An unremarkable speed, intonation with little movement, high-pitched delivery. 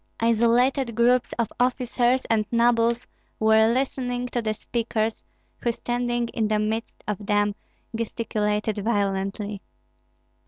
No: slow, 115 wpm; narrow, 2.2 semitones; high, 230 Hz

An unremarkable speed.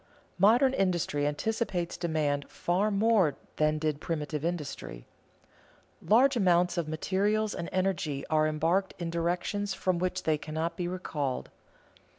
No: slow, 130 wpm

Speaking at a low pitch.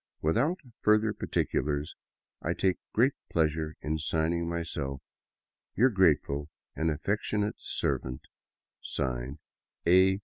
Yes: very low, 80 Hz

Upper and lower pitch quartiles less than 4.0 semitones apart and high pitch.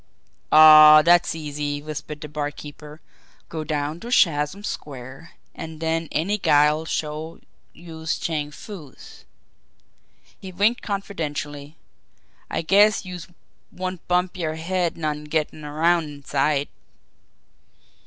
No: average, 2.7 semitones; medium, 155 Hz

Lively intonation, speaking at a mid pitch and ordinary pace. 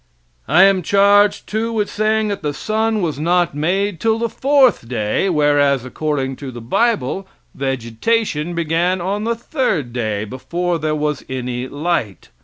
Yes: wide, 7.5 semitones; medium, 170 Hz; average, 155 wpm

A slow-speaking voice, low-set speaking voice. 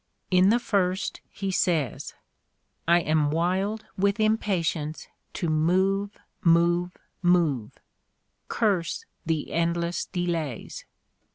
No: slow, 105 wpm; medium, 175 Hz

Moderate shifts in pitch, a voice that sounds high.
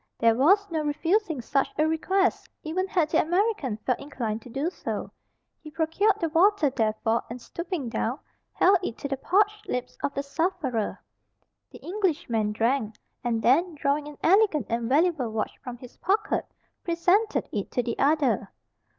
No: wide, 6.9 semitones; very high, 295 Hz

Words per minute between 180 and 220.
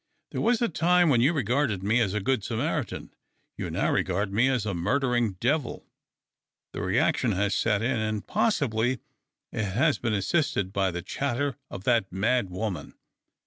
No: average, 170 wpm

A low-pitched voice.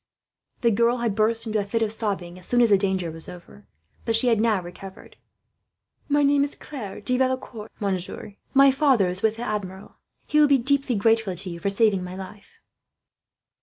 No: high, 215 Hz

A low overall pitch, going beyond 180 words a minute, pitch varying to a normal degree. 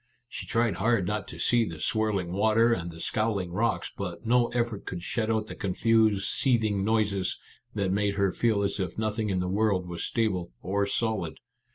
Yes: low, 105 Hz; average, 190 wpm; average, 3.1 semitones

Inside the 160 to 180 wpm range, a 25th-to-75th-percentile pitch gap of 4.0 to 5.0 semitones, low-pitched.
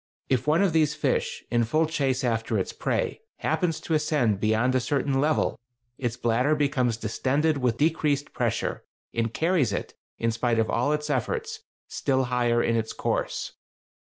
Yes: average, 170 wpm; average, 4.6 semitones; low, 130 Hz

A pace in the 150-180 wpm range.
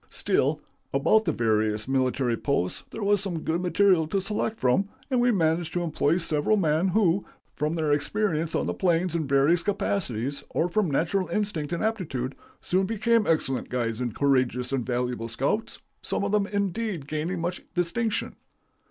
Yes: average, 170 wpm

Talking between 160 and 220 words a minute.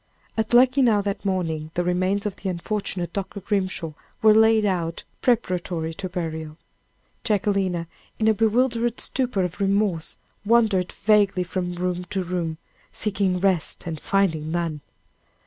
No: slow, 135 wpm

